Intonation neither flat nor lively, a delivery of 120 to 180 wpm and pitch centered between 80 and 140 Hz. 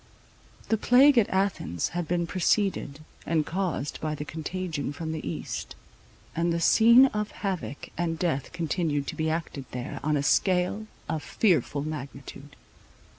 No: average, 4.1 semitones; average, 150 wpm; medium, 165 Hz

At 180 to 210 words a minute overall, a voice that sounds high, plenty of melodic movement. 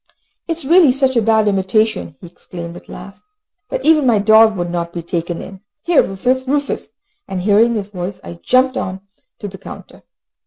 Yes: average, 190 wpm; high, 210 Hz; wide, 5.9 semitones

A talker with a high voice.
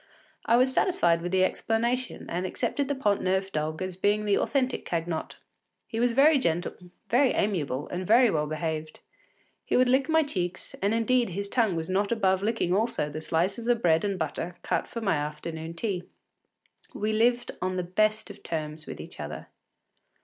Yes: high, 195 Hz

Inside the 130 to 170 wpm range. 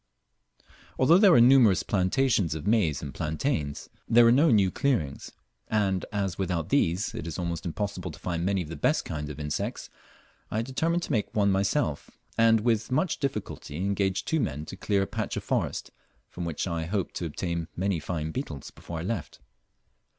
No: average, 185 wpm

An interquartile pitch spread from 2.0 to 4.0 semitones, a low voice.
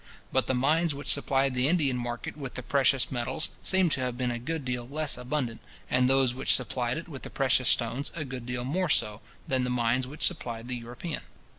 Yes: narrow, 2.6 semitones; low, 130 Hz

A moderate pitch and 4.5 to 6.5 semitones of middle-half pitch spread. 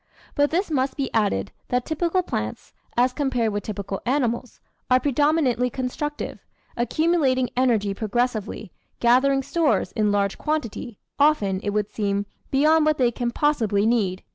No: very high, 250 Hz; wide, 5.5 semitones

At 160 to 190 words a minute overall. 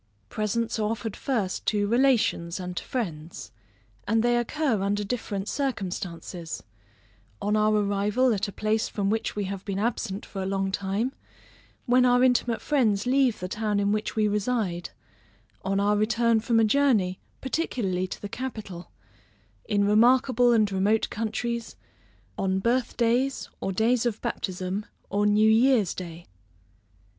No: average, 150 wpm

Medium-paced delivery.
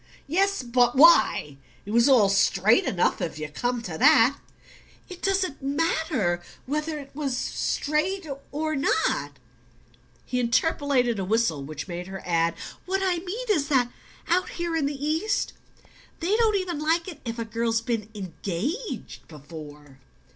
Yes: average, 155 wpm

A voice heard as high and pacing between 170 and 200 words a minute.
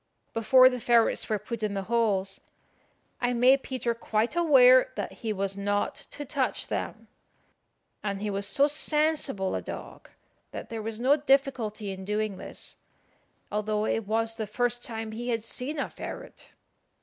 No: high, 225 Hz; average, 160 wpm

